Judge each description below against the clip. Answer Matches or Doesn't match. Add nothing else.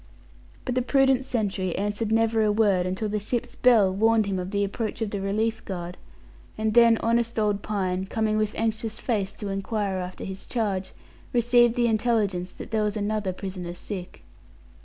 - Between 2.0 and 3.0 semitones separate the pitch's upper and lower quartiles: Matches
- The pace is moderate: Matches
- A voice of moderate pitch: Doesn't match